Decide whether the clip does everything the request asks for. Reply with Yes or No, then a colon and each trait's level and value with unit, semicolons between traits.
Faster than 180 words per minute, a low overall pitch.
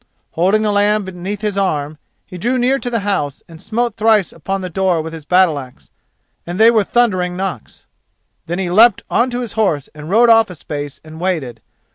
No: fast, 205 wpm; high, 190 Hz